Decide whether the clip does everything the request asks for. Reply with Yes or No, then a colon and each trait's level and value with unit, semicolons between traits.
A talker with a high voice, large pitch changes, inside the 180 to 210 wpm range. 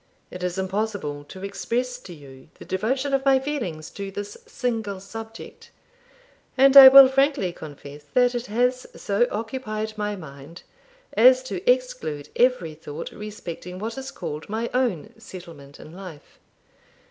No: high, 210 Hz; wide, 6.7 semitones; average, 145 wpm